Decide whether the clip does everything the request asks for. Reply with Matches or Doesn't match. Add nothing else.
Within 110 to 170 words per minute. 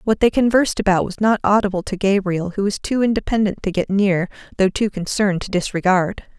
Doesn't match